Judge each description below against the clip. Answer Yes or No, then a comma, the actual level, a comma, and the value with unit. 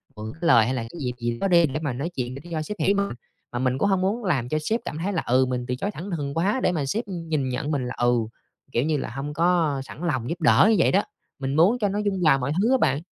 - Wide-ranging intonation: Yes, wide, 6.1 semitones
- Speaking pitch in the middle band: Yes, medium, 150 Hz